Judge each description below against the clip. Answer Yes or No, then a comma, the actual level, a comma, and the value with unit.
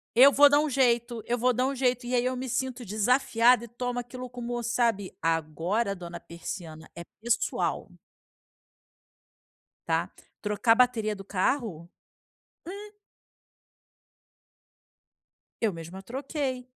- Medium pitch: No, high, 240 Hz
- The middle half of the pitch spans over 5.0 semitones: No, average, 4.0 semitones